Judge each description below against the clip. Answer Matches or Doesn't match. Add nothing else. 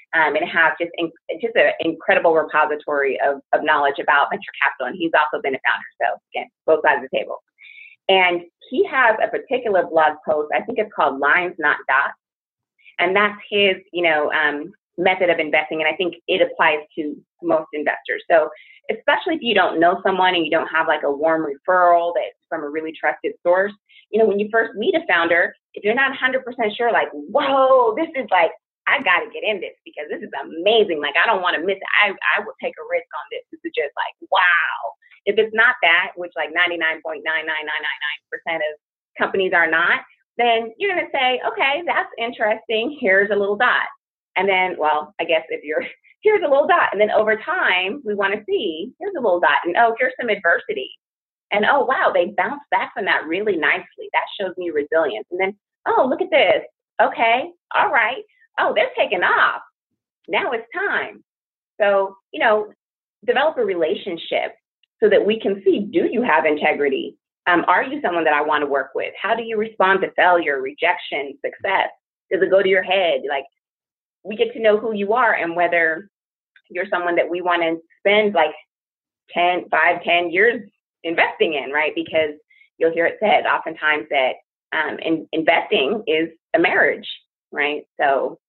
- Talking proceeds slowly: Doesn't match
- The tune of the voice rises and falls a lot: Matches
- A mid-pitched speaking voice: Doesn't match